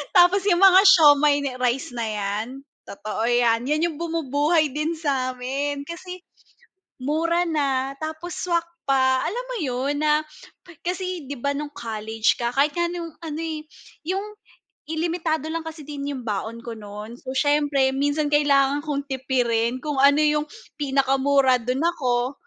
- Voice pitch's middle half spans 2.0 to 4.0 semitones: Yes, average, 3.6 semitones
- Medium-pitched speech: No, very high, 285 Hz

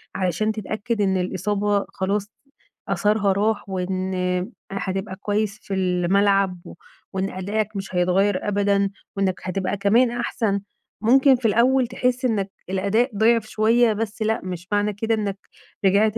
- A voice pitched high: Yes, high, 205 Hz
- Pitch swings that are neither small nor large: No, narrow, 2.3 semitones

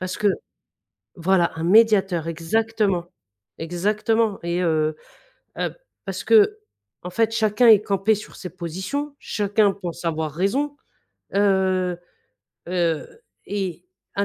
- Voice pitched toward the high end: Yes, high, 195 Hz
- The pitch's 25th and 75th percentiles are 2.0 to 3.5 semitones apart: No, average, 3.9 semitones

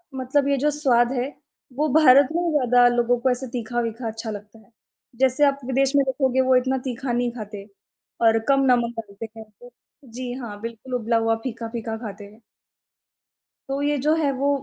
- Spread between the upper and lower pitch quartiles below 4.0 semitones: Yes, average, 3.0 semitones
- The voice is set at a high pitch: Yes, high, 245 Hz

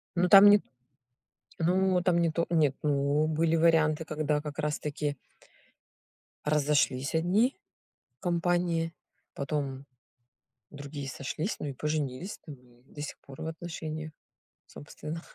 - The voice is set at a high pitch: No, medium, 155 Hz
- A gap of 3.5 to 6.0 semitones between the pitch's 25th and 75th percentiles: No, narrow, 2.6 semitones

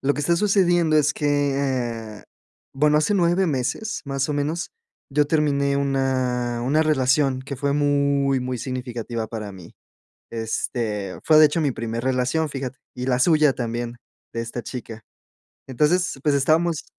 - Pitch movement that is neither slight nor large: Yes, average, 3.6 semitones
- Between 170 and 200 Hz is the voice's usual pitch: No, low, 135 Hz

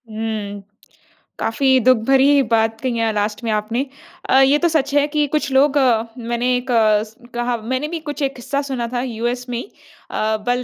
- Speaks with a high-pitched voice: Yes, high, 245 Hz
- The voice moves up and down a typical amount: Yes, average, 3.2 semitones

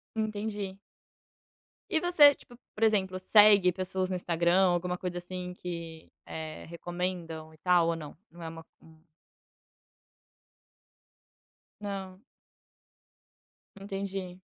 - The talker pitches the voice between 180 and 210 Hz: Yes, medium, 185 Hz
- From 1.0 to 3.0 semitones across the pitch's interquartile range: Yes, narrow, 2.5 semitones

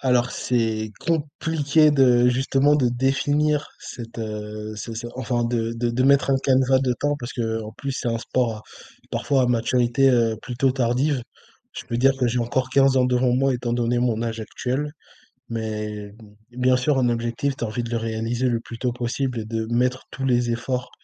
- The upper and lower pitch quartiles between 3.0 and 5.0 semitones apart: No, narrow, 2.4 semitones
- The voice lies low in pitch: Yes, low, 125 Hz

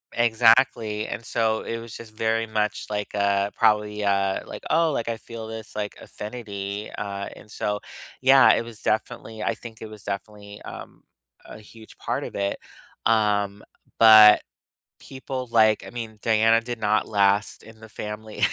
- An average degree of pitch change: No, narrow, 1.5 semitones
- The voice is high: No, low, 110 Hz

